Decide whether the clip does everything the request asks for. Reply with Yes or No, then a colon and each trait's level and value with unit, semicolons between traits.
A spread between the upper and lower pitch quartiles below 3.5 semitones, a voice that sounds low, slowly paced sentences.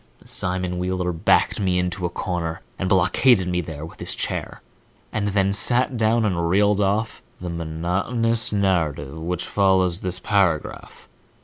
No: average, 2.9 semitones; very low, 90 Hz; average, 150 wpm